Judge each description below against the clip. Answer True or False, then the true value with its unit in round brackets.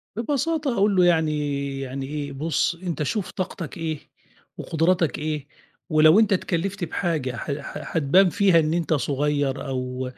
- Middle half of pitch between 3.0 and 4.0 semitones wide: False (4.4 semitones)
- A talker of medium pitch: True (155 Hz)